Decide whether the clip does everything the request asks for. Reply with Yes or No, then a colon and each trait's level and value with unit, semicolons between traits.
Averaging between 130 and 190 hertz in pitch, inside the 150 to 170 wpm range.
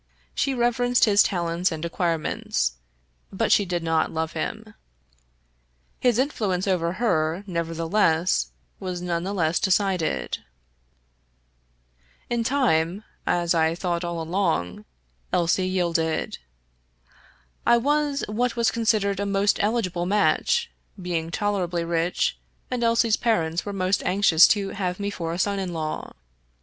No: medium, 185 Hz; slow, 135 wpm